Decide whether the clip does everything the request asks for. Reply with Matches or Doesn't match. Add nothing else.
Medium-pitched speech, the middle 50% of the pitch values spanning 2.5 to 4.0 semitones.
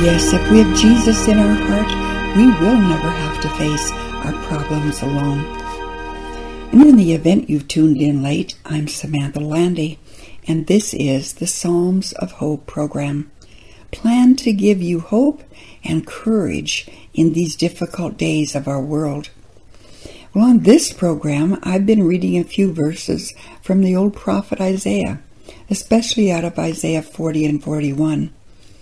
Doesn't match